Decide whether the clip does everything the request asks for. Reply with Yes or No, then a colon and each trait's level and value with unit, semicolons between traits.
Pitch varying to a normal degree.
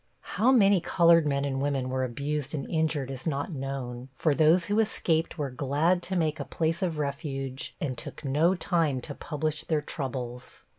Yes: average, 3.5 semitones